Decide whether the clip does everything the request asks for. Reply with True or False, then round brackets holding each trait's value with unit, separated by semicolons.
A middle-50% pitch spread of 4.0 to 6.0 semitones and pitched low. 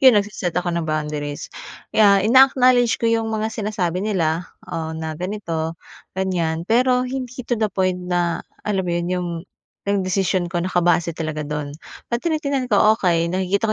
False (4.6 semitones; 185 Hz)